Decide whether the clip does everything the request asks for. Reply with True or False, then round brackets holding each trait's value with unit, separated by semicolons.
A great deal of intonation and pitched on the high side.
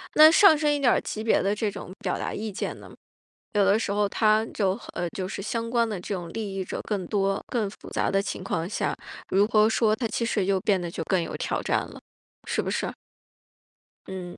False (2.8 semitones; 205 Hz)